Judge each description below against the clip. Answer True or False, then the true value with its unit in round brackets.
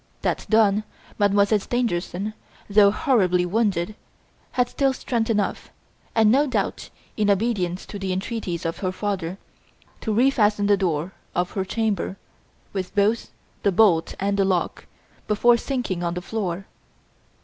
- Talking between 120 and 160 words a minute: True (140 wpm)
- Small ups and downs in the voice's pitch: False (3.2 semitones)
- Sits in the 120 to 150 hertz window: False (200 Hz)